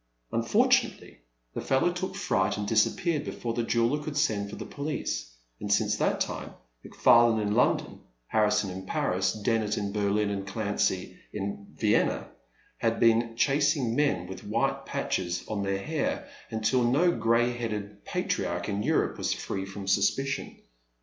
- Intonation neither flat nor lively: Yes, average, 3.6 semitones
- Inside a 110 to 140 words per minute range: No, average, 155 wpm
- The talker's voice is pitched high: No, low, 110 Hz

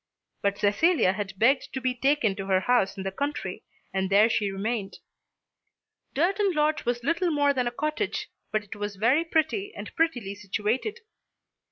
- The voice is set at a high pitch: Yes, high, 245 Hz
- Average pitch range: No, wide, 7.2 semitones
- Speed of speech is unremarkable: Yes, average, 170 wpm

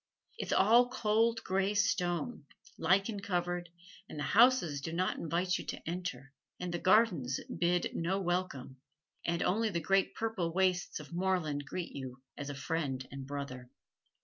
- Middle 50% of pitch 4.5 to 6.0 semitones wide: Yes, average, 5.0 semitones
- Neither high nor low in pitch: Yes, medium, 175 Hz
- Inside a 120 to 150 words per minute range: No, average, 160 wpm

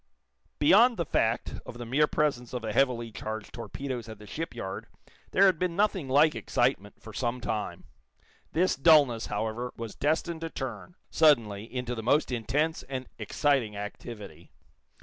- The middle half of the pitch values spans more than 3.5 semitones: Yes, average, 5.3 semitones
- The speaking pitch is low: Yes, low, 125 Hz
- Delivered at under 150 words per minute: No, average, 155 wpm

